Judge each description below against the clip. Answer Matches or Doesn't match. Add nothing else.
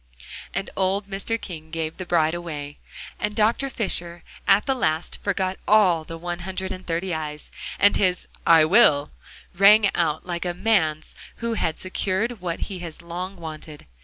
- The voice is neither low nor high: Matches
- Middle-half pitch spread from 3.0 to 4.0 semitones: Matches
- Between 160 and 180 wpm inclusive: Matches